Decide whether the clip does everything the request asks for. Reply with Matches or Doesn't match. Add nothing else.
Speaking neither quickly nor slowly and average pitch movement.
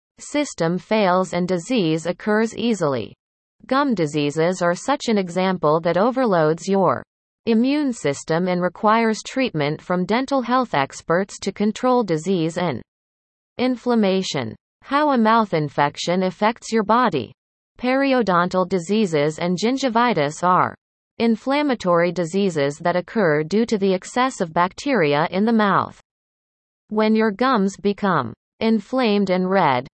Doesn't match